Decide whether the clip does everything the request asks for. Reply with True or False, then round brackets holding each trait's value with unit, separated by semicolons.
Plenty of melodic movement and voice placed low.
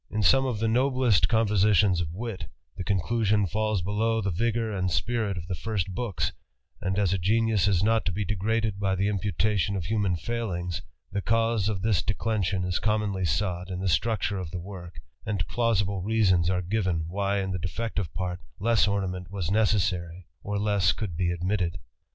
False (3.1 semitones; 100 Hz)